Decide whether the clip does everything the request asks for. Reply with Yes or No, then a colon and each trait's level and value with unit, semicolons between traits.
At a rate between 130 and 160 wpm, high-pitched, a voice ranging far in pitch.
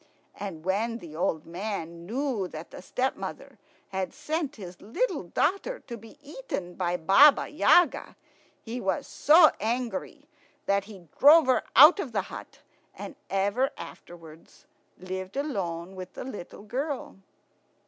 Yes: average, 140 wpm; high, 215 Hz; wide, 7.3 semitones